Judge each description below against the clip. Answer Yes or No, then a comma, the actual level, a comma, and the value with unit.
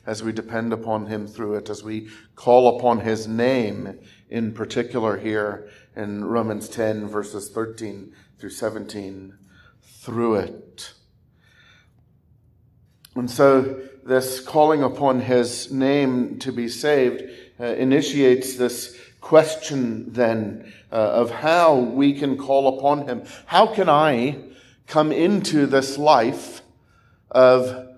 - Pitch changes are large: No, average, 3.4 semitones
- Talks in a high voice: No, low, 125 Hz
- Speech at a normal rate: No, slow, 115 wpm